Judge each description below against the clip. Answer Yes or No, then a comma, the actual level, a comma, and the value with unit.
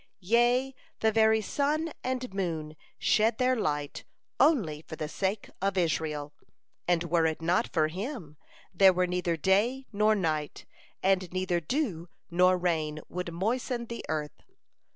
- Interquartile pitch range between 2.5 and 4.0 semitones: No, wide, 5.4 semitones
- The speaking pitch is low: No, medium, 185 Hz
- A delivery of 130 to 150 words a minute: Yes, average, 145 wpm